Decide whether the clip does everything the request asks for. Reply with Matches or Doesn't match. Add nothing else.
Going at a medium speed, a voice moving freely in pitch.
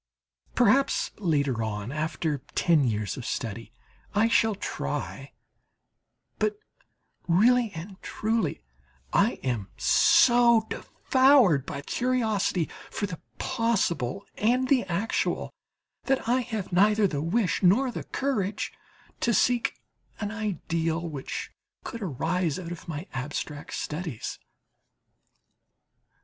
Doesn't match